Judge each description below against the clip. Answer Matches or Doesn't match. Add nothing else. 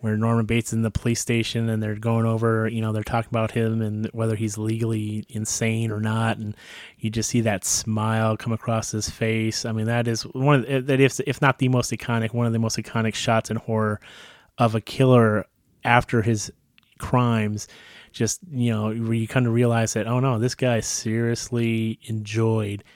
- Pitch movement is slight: Matches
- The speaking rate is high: Doesn't match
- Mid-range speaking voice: Doesn't match